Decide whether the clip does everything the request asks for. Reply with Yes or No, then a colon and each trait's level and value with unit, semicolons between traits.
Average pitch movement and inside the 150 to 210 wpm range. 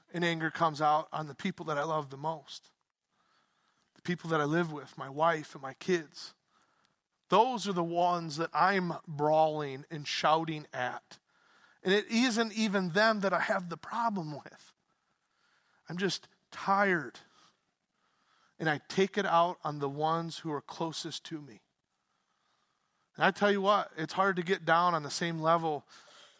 Yes: average, 3.9 semitones; average, 170 wpm